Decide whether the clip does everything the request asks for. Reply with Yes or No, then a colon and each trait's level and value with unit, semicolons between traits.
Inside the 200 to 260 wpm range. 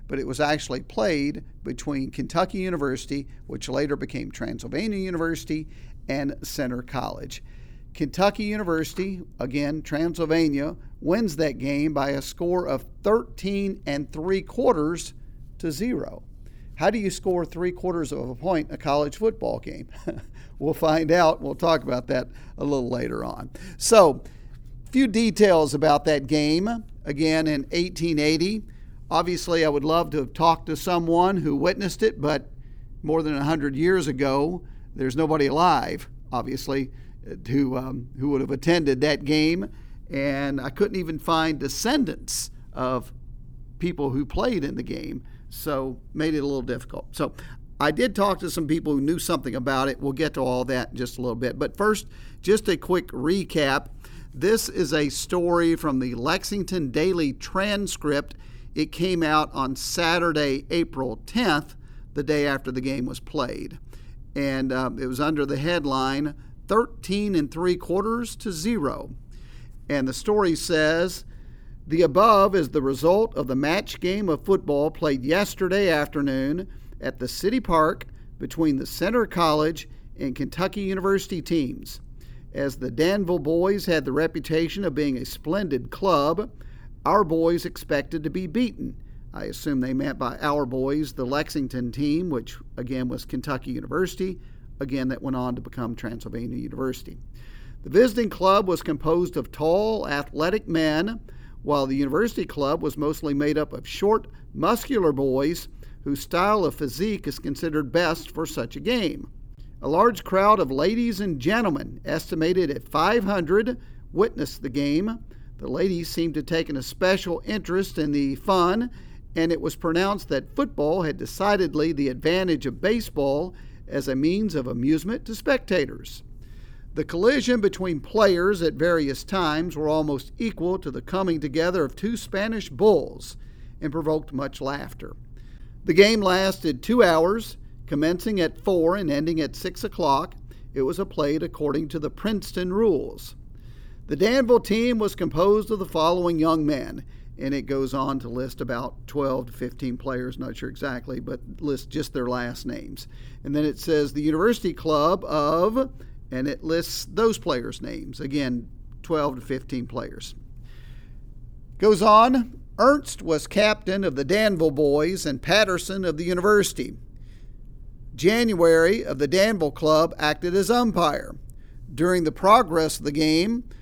No: average, 155 wpm